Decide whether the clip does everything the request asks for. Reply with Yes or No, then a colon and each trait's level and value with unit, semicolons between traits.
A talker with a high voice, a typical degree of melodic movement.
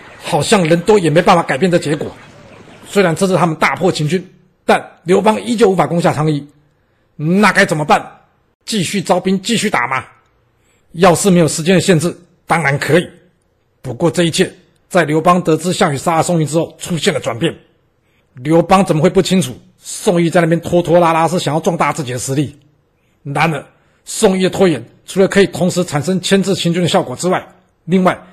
No: medium, 170 Hz; average, 3.6 semitones